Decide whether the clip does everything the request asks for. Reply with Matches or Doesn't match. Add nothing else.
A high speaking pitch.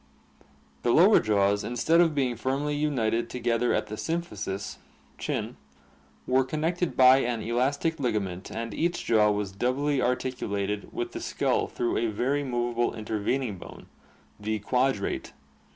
Doesn't match